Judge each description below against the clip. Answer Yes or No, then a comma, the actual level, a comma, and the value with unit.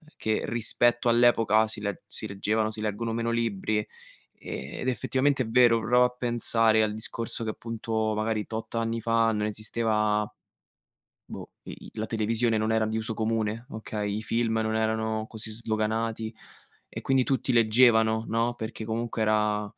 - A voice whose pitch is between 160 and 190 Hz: No, low, 110 Hz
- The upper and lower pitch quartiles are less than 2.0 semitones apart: Yes, narrow, 1.1 semitones